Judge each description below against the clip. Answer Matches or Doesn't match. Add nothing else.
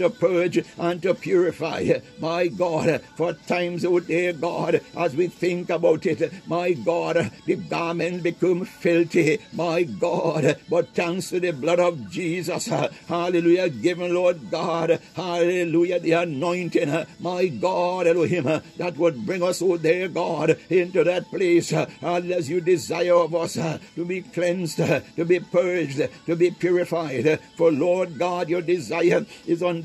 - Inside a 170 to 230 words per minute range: Doesn't match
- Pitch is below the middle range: Doesn't match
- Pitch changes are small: Matches